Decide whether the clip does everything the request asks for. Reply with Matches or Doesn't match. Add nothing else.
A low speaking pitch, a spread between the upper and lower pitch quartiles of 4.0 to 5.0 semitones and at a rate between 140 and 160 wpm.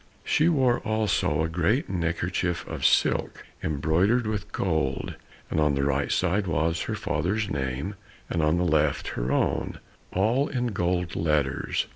Doesn't match